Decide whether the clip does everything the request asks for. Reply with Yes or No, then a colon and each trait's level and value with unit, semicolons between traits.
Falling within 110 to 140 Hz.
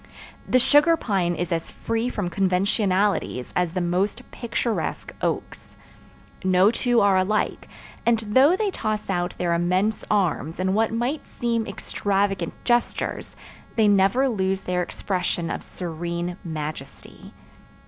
No: high, 195 Hz